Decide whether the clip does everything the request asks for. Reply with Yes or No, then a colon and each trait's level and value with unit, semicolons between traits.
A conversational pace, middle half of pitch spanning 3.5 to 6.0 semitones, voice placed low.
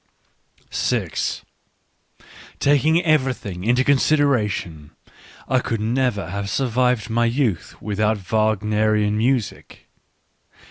No: slow, 85 wpm; average, 3.8 semitones; low, 115 Hz